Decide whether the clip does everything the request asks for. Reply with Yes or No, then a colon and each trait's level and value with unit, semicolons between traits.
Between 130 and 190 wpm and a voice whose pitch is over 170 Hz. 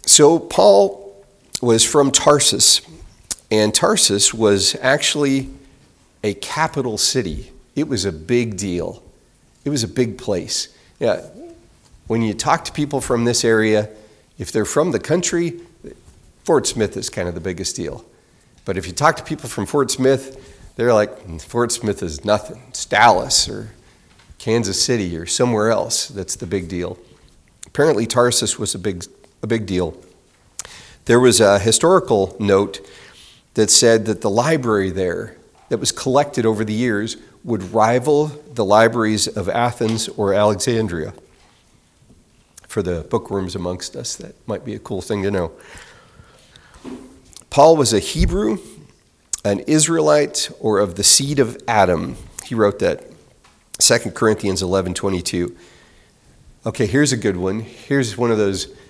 No: average, 150 wpm; low, 110 Hz